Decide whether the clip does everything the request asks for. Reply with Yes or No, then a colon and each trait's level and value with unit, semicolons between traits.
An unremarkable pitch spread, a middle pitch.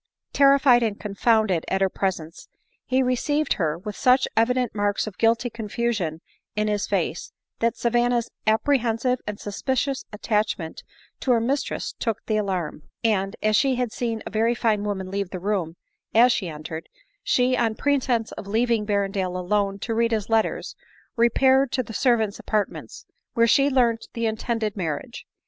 No: average, 3.2 semitones; high, 220 Hz